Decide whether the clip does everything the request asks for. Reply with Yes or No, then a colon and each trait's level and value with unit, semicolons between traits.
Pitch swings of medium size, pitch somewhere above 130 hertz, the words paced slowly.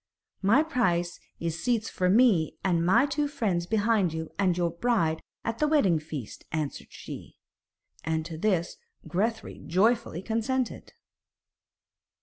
No: wide, 5.7 semitones; high, 190 Hz; slow, 130 wpm